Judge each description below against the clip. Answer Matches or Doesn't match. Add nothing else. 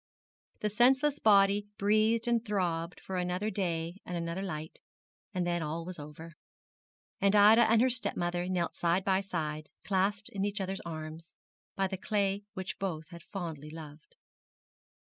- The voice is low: Doesn't match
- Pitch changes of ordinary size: Matches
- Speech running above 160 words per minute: Doesn't match